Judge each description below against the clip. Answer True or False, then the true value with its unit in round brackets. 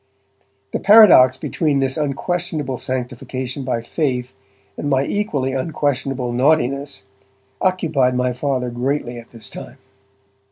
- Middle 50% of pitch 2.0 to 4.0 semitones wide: True (2.8 semitones)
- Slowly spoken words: True (115 wpm)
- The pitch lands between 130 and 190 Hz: True (135 Hz)